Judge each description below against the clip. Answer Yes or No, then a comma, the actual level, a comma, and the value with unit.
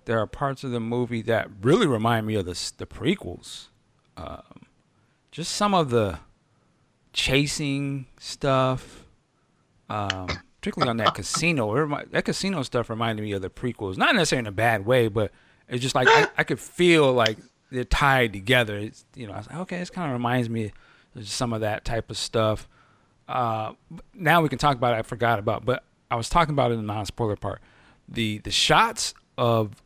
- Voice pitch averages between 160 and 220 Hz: No, low, 120 Hz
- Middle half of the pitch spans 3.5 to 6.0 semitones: Yes, average, 4.2 semitones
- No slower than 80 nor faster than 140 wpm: No, average, 195 wpm